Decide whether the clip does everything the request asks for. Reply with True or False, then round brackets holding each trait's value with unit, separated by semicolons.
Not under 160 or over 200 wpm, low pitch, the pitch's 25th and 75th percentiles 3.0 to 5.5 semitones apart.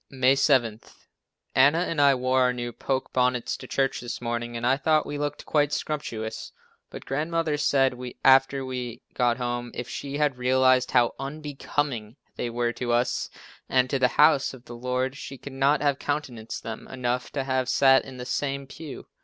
False (180 wpm; 130 Hz; 2.5 semitones)